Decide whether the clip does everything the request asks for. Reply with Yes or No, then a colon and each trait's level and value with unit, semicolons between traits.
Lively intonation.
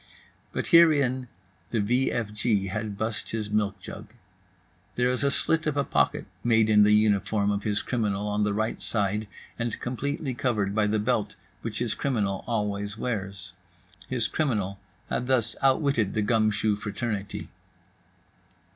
No: average, 3.1 semitones